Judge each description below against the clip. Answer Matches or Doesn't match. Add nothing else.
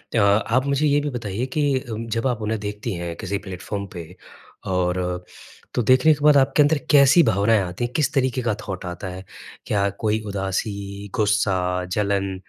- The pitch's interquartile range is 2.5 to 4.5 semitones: Doesn't match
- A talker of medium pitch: Doesn't match